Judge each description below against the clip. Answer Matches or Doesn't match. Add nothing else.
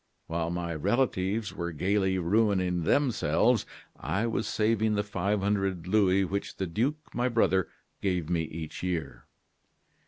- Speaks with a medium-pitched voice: Doesn't match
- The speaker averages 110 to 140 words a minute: Matches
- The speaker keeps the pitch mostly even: Doesn't match